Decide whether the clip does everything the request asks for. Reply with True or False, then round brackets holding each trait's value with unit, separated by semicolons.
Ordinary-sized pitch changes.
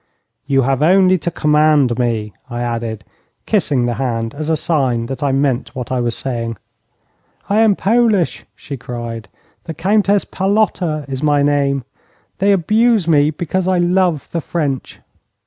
False (6.6 semitones)